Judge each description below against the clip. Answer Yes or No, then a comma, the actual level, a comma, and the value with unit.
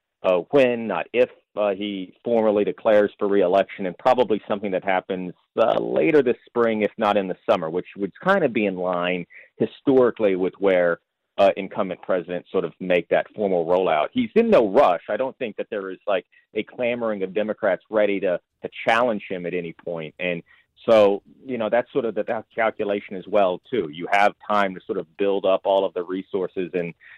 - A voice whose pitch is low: Yes, low, 100 Hz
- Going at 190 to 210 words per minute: Yes, fast, 205 wpm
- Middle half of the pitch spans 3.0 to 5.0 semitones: Yes, average, 3.4 semitones